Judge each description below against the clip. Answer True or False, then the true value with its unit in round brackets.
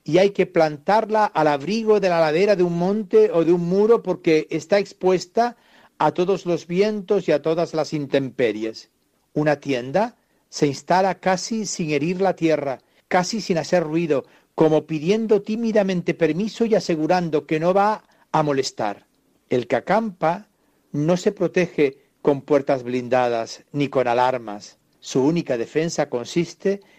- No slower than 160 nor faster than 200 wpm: False (150 wpm)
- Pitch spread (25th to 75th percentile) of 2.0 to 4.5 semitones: False (4.9 semitones)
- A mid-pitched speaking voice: True (170 Hz)